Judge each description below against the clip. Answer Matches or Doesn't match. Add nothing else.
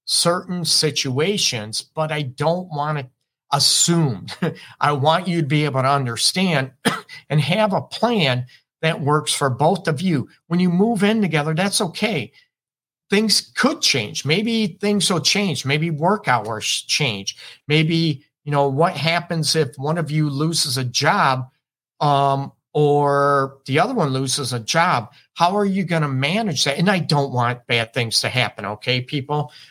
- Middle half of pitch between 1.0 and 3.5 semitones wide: Doesn't match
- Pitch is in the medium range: Matches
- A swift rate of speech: Doesn't match